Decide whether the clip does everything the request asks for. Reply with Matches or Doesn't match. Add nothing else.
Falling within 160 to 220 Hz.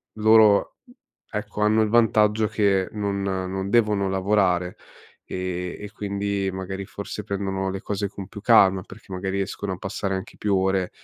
Doesn't match